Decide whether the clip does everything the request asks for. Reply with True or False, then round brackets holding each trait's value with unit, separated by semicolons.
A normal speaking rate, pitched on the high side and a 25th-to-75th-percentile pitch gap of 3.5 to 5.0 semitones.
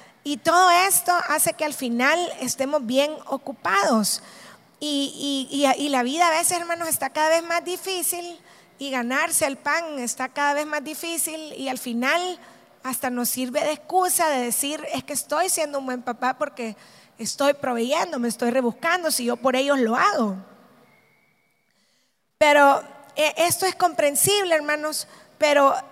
True (155 wpm; 290 Hz; 4.1 semitones)